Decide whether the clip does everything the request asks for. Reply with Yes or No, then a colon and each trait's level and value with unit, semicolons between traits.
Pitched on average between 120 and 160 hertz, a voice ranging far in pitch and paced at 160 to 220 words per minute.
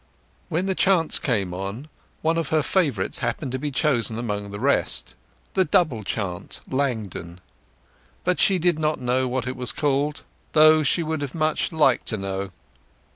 Yes: low, 135 Hz; wide, 6.2 semitones; average, 165 wpm